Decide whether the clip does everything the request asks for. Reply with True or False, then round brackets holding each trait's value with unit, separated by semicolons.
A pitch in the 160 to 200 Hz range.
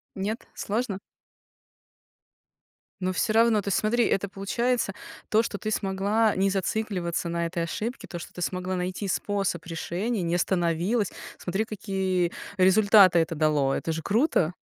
True (190 Hz)